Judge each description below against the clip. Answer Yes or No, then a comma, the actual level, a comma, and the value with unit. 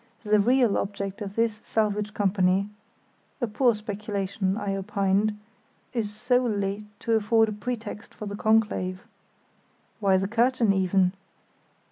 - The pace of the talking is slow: Yes, slow, 125 wpm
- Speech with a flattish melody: Yes, narrow, 2.1 semitones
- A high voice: Yes, high, 210 Hz